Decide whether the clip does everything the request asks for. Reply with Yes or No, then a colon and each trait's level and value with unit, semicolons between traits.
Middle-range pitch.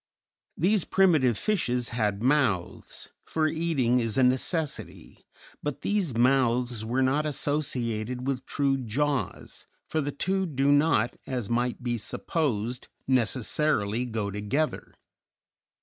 No: low, 130 Hz